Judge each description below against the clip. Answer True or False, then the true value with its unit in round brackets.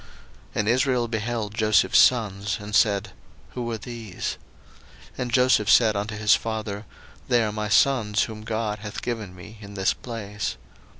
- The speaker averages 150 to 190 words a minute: True (165 wpm)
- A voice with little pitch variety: True (2.2 semitones)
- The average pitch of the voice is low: True (110 Hz)